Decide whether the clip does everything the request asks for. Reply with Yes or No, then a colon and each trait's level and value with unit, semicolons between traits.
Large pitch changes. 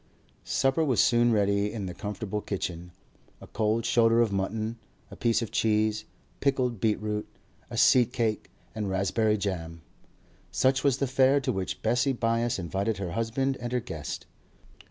No: average, 3.2 semitones